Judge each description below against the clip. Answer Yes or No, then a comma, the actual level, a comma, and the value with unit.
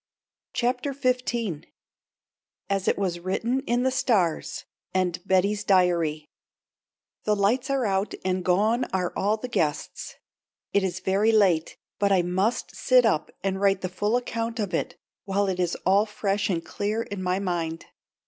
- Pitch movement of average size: Yes, average, 3.7 semitones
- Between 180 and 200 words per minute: No, average, 160 wpm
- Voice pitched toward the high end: Yes, high, 200 Hz